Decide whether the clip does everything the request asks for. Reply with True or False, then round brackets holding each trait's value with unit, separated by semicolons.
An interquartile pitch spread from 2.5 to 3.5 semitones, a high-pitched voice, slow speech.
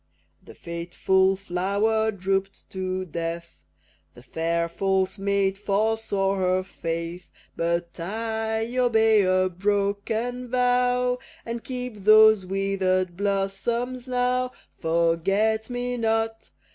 True (3.2 semitones; 200 Hz; 100 wpm)